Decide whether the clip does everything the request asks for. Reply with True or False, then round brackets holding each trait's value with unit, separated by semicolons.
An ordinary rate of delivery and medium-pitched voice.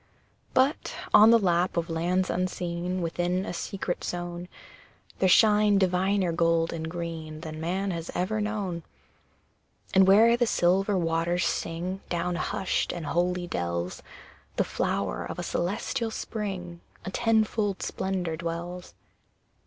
False (130 wpm; 180 Hz)